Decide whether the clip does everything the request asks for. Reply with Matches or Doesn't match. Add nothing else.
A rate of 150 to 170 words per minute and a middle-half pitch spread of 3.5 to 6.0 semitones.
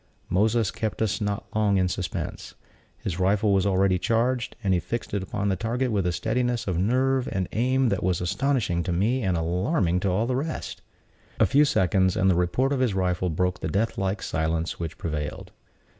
Doesn't match